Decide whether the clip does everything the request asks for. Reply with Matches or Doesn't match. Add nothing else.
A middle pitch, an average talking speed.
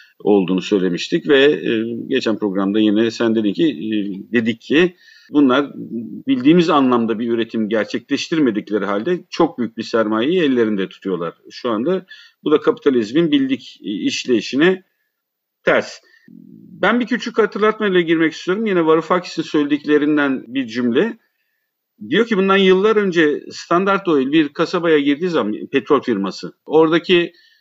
Matches